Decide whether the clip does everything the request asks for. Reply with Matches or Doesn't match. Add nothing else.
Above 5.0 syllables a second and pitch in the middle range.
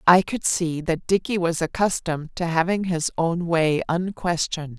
Doesn't match